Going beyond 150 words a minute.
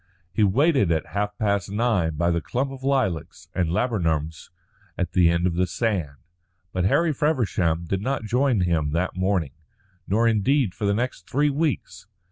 Yes: average, 170 wpm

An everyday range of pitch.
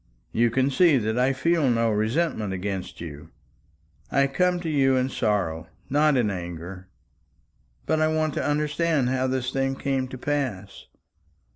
No: wide, 5.8 semitones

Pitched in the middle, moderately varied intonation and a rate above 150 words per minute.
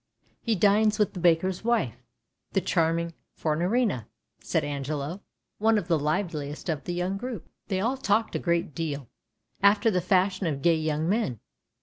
Yes: medium, 175 Hz; average, 4.8 semitones; average, 165 wpm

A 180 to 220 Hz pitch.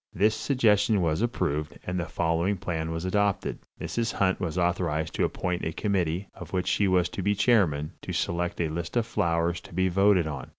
No: very low, 90 Hz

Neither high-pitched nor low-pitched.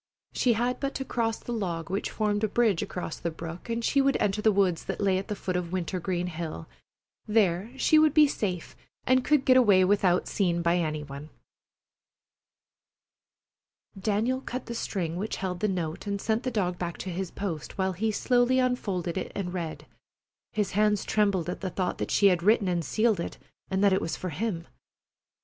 No: high, 195 Hz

